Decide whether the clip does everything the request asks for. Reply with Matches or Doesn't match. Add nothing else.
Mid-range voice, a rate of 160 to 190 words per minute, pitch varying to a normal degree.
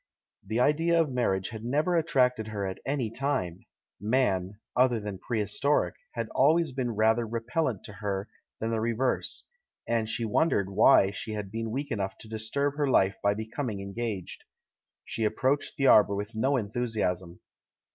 Doesn't match